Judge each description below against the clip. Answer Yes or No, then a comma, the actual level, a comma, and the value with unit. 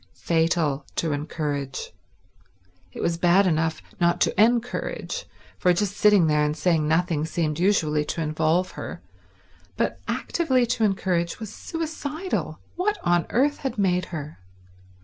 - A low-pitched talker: No, medium, 175 Hz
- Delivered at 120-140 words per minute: Yes, slow, 135 wpm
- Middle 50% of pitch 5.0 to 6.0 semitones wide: Yes, wide, 5.4 semitones